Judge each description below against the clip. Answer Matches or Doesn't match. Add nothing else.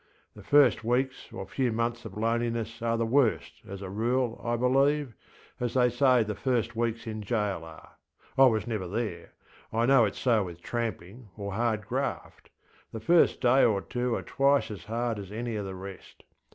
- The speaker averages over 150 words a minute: Matches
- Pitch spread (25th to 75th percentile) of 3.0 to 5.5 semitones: Doesn't match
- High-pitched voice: Doesn't match